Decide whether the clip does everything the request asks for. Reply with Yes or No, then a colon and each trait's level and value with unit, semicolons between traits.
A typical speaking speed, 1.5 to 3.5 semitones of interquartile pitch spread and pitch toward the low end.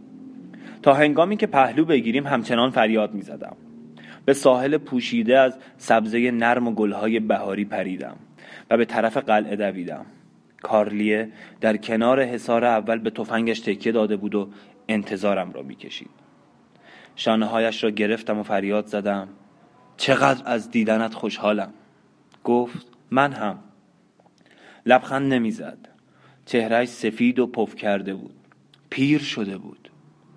Yes: average, 125 wpm; average, 3.0 semitones; low, 115 Hz